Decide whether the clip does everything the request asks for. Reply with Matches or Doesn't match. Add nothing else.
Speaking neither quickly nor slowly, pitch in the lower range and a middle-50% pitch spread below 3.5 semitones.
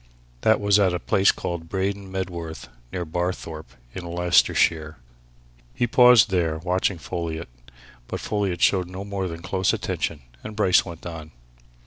Matches